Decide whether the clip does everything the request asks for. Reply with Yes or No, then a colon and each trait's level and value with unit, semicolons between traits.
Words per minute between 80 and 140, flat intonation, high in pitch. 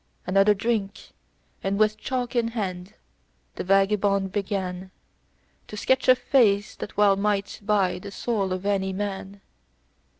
Yes: slow, 135 wpm; narrow, 1.7 semitones; high, 200 Hz